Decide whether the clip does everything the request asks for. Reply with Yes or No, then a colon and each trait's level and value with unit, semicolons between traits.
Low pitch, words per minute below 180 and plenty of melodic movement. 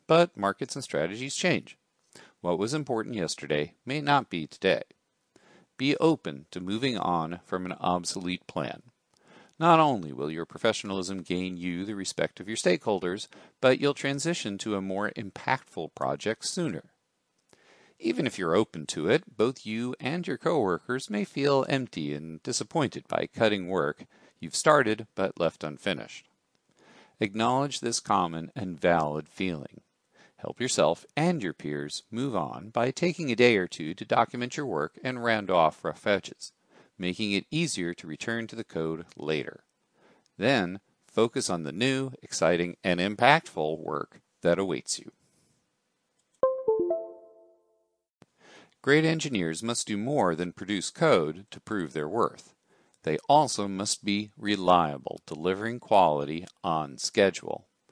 Yes: low, 110 Hz; average, 140 wpm; wide, 6.8 semitones